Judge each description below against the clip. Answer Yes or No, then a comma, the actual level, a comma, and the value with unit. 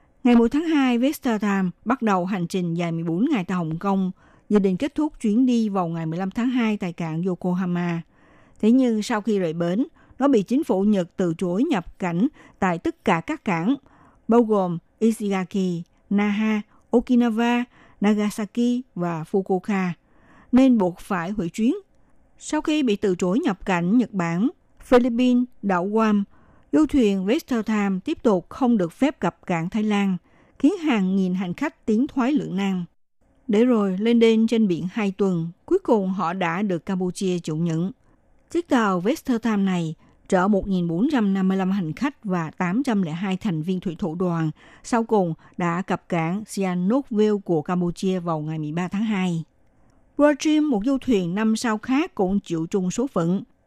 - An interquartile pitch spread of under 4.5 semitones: No, average, 4.9 semitones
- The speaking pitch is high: Yes, high, 205 Hz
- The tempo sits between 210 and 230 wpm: No, average, 170 wpm